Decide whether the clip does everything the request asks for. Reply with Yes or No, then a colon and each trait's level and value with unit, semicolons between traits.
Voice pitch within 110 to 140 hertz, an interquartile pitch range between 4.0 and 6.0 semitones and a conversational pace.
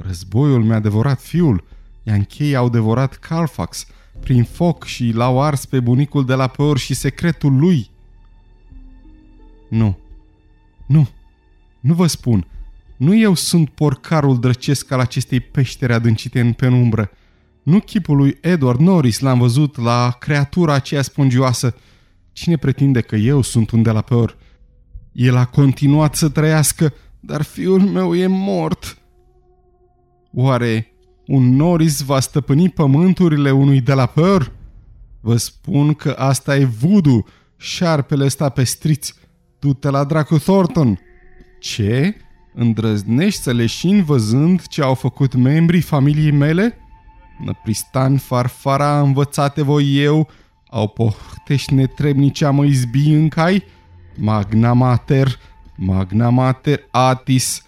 Yes: low, 130 Hz; average, 4.5 semitones; average, 125 wpm